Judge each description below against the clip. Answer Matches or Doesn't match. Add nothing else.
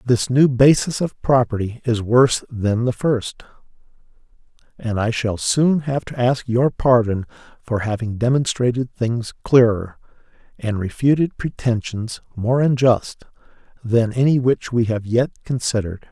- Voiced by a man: Matches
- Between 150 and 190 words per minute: Doesn't match